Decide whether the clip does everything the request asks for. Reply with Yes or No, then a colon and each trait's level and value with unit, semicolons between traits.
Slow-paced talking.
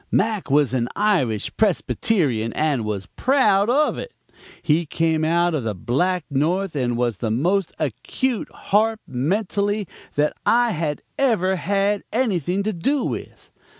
No: average, 145 wpm